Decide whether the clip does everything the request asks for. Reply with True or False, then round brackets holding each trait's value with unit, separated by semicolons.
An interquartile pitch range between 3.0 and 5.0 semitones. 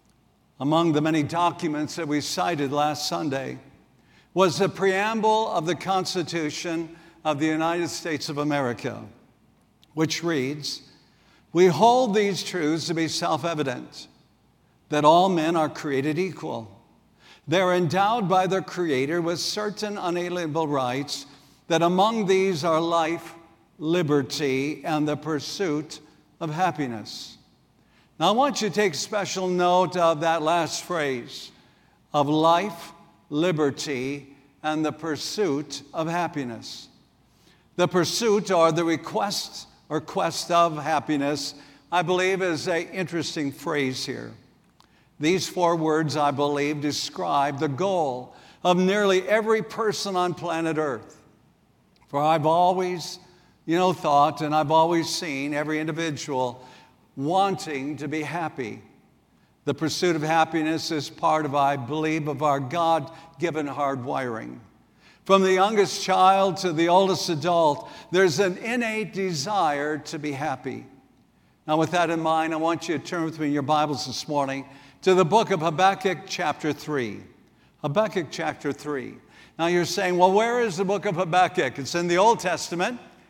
True (3.6 semitones)